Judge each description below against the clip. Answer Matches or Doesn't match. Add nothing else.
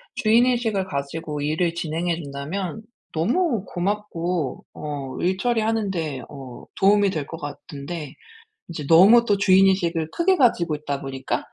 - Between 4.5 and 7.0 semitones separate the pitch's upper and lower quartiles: Matches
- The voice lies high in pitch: Doesn't match